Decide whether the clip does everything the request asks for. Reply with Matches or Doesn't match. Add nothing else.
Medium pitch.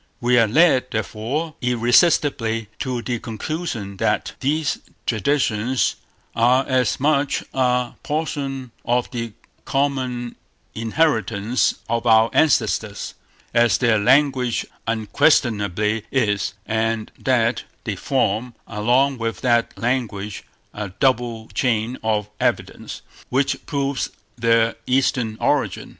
Doesn't match